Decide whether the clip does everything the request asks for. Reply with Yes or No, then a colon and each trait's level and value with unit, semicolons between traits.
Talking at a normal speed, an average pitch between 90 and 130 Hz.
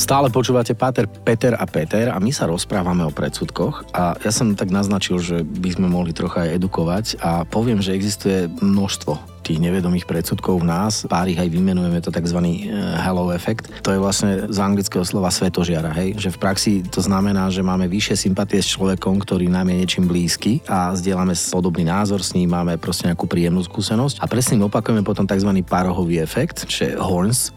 No: fast, 190 wpm; very low, 95 Hz